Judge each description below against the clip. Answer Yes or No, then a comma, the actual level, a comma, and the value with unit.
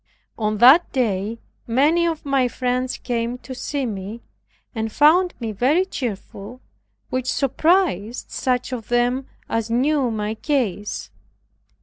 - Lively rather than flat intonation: No, average, 3.7 semitones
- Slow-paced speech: Yes, slow, 125 wpm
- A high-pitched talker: Yes, very high, 250 Hz